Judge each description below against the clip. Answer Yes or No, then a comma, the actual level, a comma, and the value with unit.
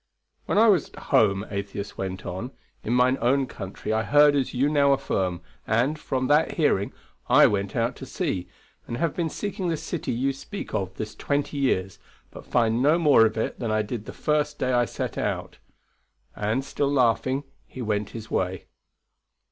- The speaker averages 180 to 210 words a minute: Yes, average, 190 wpm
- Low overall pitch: Yes, low, 125 Hz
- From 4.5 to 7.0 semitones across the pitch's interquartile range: Yes, wide, 5.4 semitones